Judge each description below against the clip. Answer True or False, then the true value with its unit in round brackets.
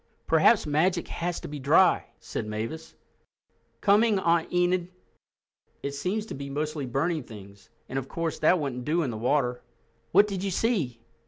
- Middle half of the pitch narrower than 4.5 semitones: False (5.0 semitones)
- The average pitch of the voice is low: False (155 Hz)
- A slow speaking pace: False (165 wpm)